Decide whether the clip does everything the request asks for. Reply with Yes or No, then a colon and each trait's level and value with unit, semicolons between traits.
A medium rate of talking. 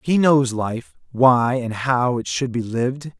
Yes: average, 190 wpm